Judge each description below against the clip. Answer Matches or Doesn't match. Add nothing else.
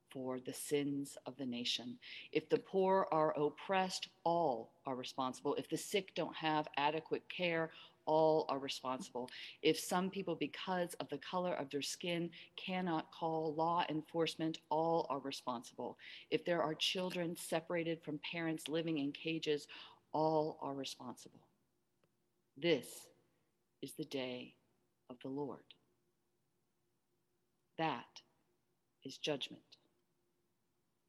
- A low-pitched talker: Doesn't match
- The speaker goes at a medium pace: Doesn't match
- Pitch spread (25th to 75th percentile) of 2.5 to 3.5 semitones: Matches